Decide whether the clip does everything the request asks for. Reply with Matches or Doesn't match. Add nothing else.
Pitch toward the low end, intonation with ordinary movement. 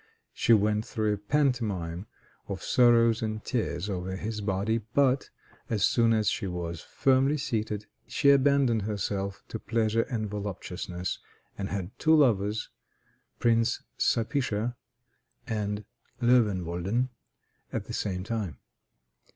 Matches